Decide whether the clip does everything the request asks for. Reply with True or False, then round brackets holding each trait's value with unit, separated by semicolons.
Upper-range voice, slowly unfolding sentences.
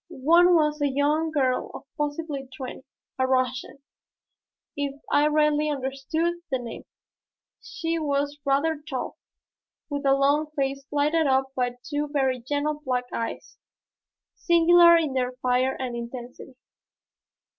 True (285 Hz; 130 wpm)